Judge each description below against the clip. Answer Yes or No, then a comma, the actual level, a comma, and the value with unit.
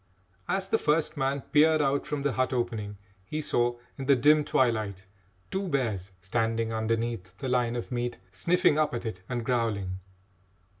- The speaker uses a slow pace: No, average, 165 wpm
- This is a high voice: No, low, 120 Hz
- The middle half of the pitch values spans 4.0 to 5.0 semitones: Yes, average, 4.3 semitones